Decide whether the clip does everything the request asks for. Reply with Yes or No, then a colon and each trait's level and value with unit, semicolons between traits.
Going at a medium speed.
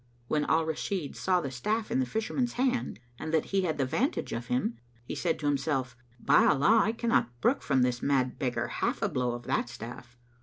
No: fast, 215 wpm